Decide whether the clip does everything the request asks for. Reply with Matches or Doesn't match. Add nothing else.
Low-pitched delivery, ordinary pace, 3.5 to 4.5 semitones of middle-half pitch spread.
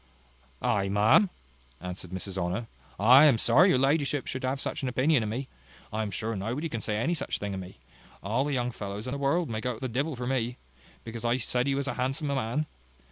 Doesn't match